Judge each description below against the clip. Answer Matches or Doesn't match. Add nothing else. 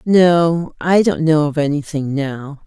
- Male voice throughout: Doesn't match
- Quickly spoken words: Doesn't match